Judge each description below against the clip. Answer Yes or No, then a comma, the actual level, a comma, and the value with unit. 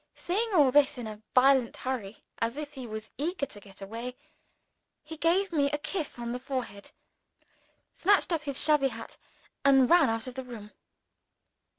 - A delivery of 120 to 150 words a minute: No, average, 175 wpm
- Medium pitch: No, very high, 265 Hz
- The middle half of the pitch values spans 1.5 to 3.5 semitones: No, average, 4.6 semitones